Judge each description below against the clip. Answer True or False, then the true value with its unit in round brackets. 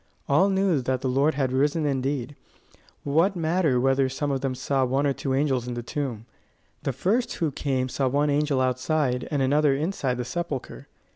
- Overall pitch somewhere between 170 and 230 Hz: False (140 Hz)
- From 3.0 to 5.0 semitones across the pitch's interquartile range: False (2.5 semitones)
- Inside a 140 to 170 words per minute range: False (190 wpm)